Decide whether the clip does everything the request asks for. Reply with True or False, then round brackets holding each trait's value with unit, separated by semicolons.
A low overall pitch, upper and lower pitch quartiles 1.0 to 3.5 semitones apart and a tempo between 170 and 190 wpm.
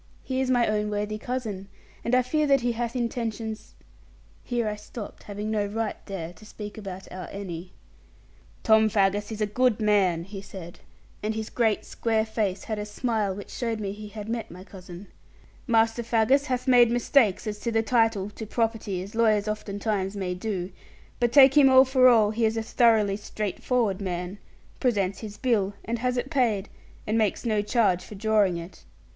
False (215 Hz; 2.7 semitones; 185 wpm)